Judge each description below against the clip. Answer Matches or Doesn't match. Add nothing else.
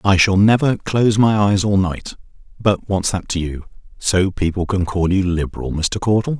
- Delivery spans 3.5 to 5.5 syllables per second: Matches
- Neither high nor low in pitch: Doesn't match